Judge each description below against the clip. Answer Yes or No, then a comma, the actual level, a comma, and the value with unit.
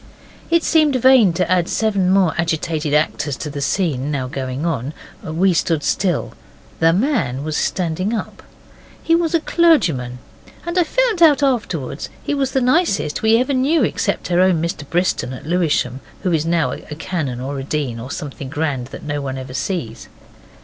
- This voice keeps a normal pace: Yes, average, 180 wpm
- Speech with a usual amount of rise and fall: No, wide, 8.1 semitones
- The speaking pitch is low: No, medium, 165 Hz